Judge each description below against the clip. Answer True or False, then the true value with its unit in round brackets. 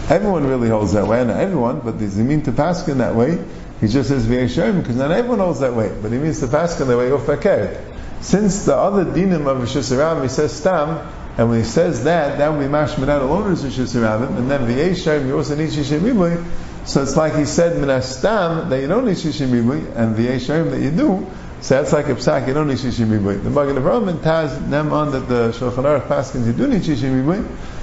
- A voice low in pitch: False (145 Hz)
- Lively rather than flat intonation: False (4.3 semitones)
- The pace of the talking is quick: True (225 wpm)